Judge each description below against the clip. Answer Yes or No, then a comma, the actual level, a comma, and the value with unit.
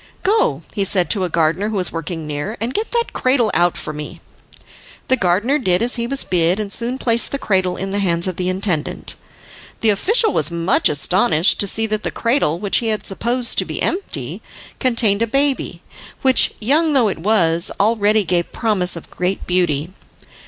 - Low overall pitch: No, high, 200 Hz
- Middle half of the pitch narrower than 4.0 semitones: No, average, 5.0 semitones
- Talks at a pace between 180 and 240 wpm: Yes, average, 195 wpm